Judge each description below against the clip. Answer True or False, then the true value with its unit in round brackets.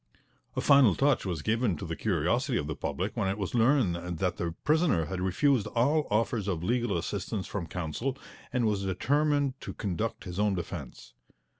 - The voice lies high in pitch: False (105 Hz)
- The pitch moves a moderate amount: False (6.1 semitones)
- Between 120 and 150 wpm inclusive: False (180 wpm)